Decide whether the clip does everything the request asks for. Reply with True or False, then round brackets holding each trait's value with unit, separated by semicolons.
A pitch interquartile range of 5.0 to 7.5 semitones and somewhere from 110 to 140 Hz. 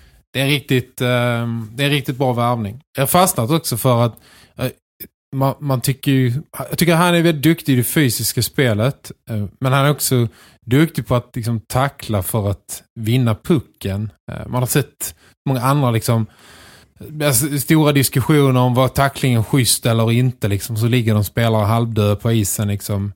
False (3.7 semitones; 125 Hz)